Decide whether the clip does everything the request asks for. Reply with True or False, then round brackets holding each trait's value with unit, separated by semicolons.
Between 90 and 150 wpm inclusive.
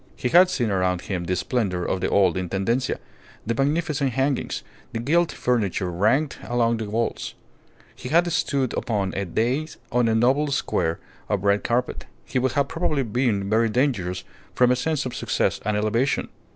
False (175 wpm)